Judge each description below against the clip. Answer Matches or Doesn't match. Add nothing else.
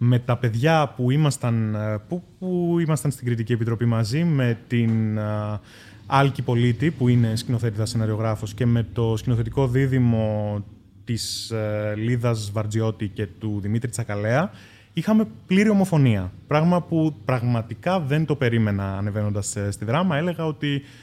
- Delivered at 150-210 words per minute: Doesn't match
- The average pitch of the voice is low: Matches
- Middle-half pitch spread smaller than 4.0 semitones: Doesn't match